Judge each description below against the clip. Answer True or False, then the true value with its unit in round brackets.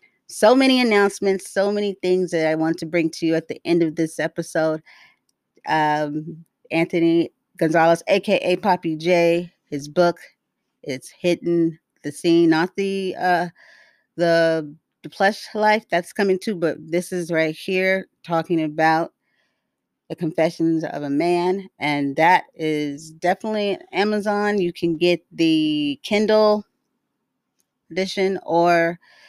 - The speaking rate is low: True (130 wpm)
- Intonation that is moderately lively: True (3.1 semitones)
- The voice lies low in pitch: False (170 Hz)